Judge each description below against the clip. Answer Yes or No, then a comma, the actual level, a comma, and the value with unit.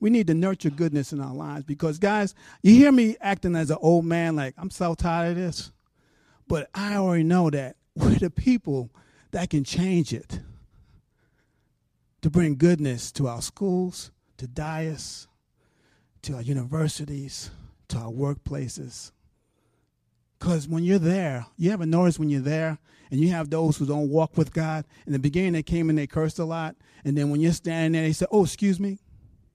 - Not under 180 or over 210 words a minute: Yes, average, 185 wpm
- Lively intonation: No, average, 3.6 semitones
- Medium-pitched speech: Yes, medium, 160 Hz